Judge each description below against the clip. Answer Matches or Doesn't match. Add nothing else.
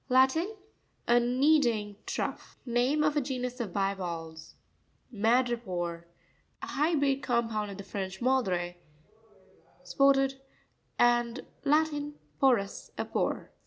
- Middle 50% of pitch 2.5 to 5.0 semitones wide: Doesn't match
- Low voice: Doesn't match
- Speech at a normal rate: Doesn't match